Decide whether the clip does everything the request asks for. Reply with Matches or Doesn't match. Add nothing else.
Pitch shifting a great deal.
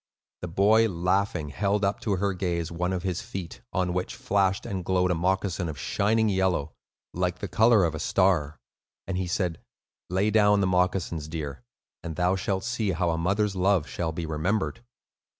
Doesn't match